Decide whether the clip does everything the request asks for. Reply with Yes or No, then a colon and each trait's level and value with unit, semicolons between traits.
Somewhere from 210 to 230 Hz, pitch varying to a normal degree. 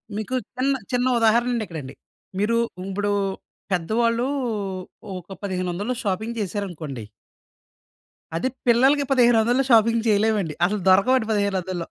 Yes: high, 215 Hz; average, 4.0 semitones